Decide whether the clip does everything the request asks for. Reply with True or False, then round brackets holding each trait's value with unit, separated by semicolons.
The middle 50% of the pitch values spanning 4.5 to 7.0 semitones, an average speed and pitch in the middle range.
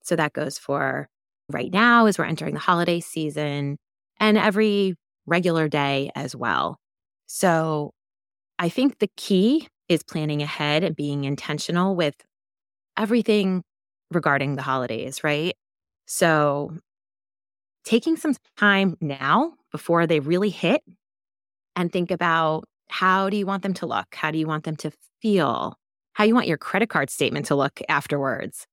True (4.8 semitones; 150 wpm; 170 Hz)